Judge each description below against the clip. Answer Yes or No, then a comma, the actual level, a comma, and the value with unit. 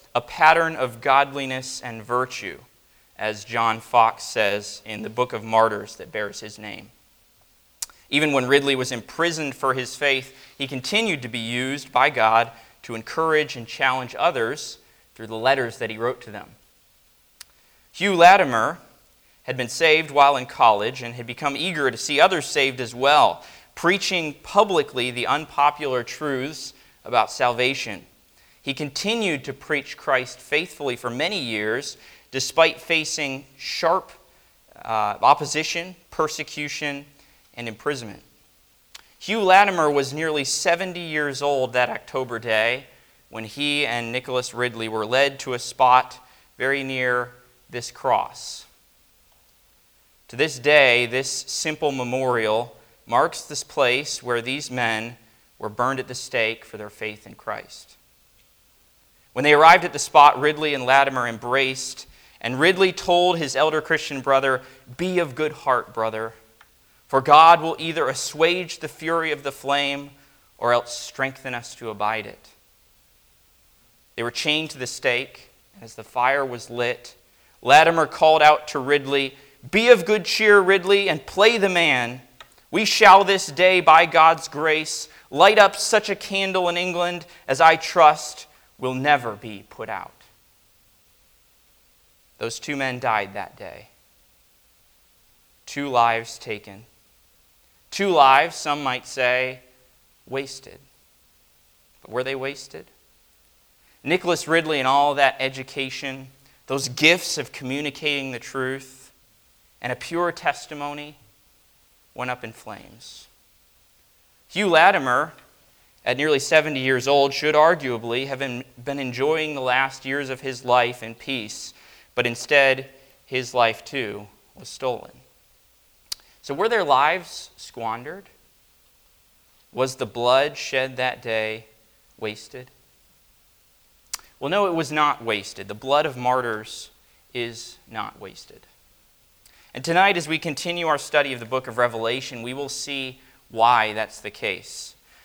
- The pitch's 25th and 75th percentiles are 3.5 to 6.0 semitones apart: Yes, average, 4.0 semitones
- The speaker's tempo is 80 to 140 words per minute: Yes, slow, 135 wpm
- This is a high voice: No, low, 135 Hz